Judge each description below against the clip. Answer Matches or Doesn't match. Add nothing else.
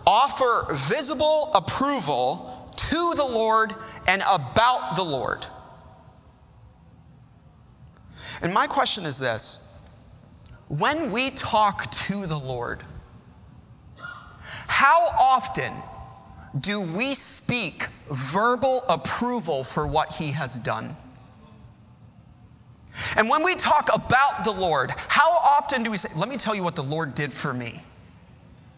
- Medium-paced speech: Doesn't match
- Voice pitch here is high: Matches